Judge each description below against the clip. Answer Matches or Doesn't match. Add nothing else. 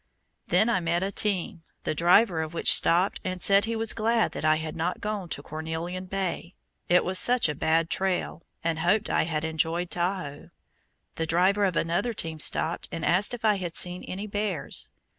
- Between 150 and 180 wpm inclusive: Doesn't match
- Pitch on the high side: Doesn't match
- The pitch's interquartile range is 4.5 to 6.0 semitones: Doesn't match